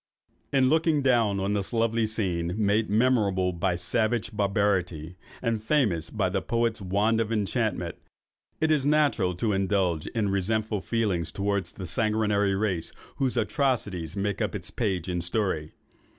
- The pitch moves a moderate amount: Yes, average, 3.6 semitones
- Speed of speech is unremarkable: Yes, average, 150 wpm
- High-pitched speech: No, low, 105 Hz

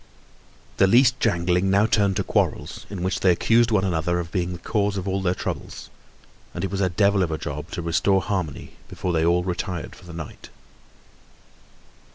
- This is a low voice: Yes, very low, 95 Hz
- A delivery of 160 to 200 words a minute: Yes, average, 195 wpm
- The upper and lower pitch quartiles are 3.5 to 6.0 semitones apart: No, narrow, 2.4 semitones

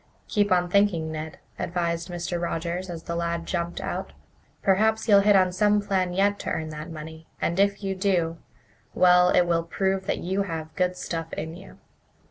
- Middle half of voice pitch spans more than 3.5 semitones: No, narrow, 2.6 semitones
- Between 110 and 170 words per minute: No, average, 185 wpm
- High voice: No, medium, 180 Hz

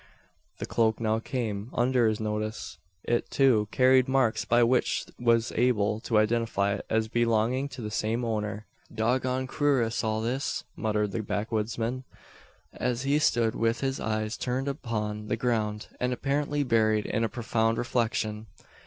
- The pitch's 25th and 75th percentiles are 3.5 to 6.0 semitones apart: No, narrow, 2.6 semitones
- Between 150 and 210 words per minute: Yes, average, 160 wpm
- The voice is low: Yes, low, 115 Hz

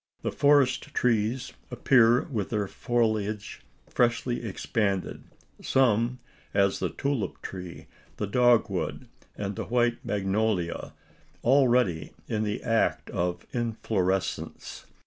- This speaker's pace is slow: Yes, slow, 105 wpm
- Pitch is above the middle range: No, low, 115 Hz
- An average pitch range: Yes, average, 3.5 semitones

